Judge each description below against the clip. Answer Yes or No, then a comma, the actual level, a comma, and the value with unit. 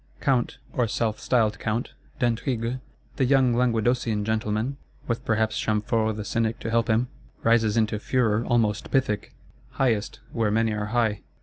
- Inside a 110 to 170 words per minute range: Yes, average, 145 wpm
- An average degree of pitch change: No, narrow, 2.0 semitones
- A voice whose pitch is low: Yes, low, 115 Hz